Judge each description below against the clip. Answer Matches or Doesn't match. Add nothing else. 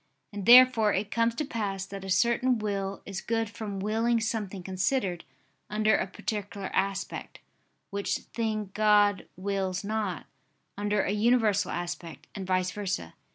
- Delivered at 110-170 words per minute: Matches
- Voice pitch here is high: Matches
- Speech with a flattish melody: Matches